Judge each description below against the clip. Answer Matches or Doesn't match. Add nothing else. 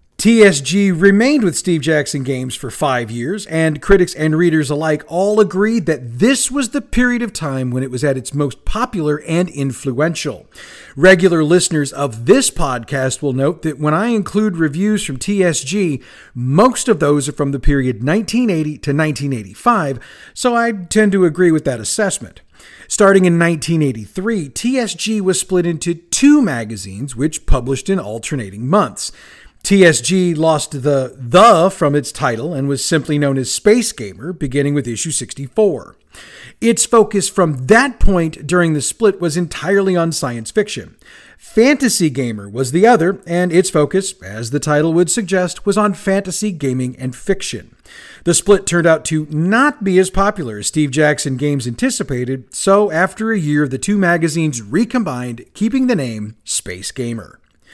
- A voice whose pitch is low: Doesn't match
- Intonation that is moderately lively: Doesn't match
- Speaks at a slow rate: Doesn't match